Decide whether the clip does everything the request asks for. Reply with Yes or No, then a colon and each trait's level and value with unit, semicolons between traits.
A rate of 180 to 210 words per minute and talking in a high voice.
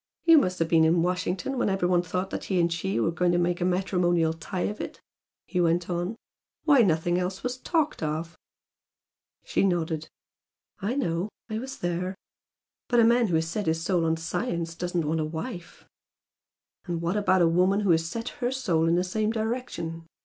No: average, 200 wpm; medium, 180 Hz